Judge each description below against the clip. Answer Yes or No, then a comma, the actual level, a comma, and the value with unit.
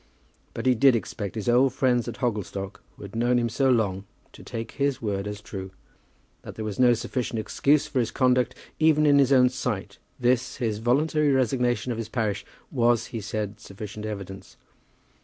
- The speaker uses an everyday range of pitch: Yes, average, 3.3 semitones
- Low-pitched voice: Yes, low, 120 Hz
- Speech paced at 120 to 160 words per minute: No, average, 185 wpm